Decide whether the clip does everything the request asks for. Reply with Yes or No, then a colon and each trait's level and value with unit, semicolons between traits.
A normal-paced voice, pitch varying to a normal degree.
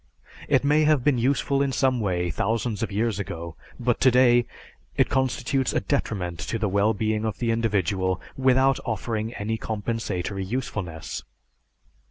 Yes: average, 150 wpm; average, 4.1 semitones